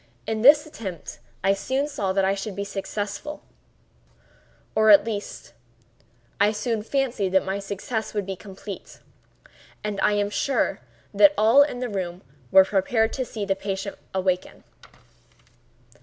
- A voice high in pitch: Yes, high, 205 Hz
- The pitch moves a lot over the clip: No, average, 2.9 semitones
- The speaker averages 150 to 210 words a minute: No, average, 140 wpm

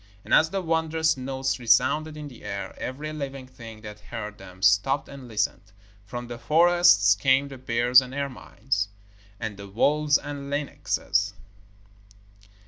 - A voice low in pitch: Yes, low, 130 Hz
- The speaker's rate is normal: Yes, average, 145 wpm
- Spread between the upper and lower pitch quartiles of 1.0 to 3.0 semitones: No, average, 5.0 semitones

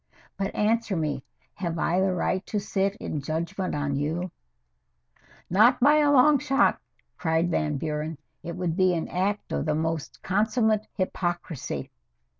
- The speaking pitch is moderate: Yes, medium, 180 Hz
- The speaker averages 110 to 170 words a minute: Yes, average, 155 wpm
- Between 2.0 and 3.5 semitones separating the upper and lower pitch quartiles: No, average, 4.5 semitones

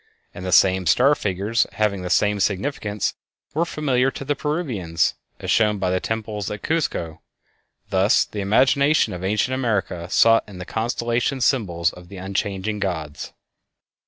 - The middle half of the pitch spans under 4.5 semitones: No, average, 5.0 semitones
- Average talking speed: Yes, average, 155 wpm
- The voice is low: Yes, low, 105 Hz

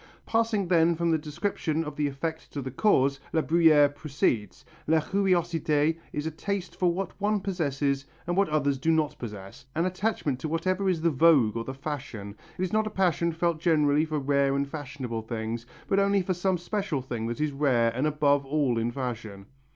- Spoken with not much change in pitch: No, average, 4.1 semitones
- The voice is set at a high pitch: No, medium, 150 Hz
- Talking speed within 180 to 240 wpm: Yes, average, 195 wpm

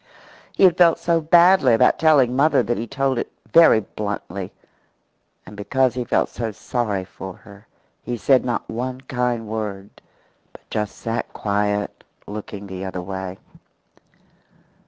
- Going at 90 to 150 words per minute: Yes, average, 145 wpm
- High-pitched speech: No, low, 115 Hz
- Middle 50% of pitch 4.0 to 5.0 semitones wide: Yes, average, 4.4 semitones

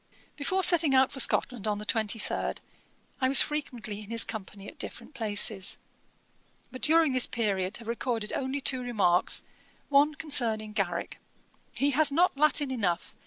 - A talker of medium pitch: No, high, 245 Hz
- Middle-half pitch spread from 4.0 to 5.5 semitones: Yes, average, 5.0 semitones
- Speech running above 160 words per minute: No, average, 155 wpm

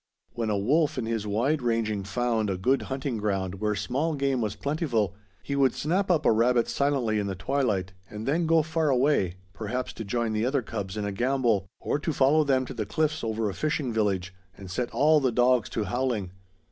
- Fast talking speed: Yes, fast, 210 wpm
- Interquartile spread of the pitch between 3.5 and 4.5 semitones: No, average, 4.9 semitones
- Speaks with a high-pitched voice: No, low, 120 Hz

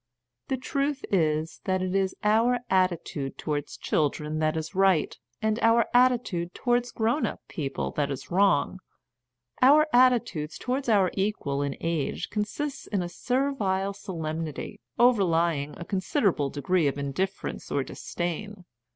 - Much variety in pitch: Yes, wide, 6.6 semitones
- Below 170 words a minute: Yes, average, 140 wpm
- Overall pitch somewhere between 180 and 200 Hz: Yes, high, 190 Hz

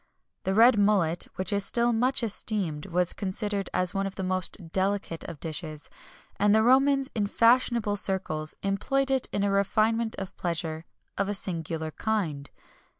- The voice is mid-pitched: No, high, 200 Hz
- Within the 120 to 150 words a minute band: No, average, 160 wpm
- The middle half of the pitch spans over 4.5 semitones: No, average, 3.9 semitones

